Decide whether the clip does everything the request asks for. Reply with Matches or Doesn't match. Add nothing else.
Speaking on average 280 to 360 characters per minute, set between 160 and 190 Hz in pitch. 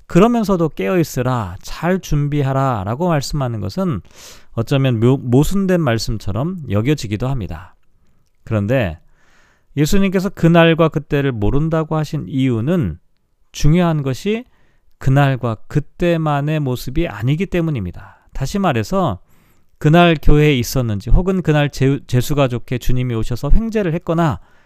Doesn't match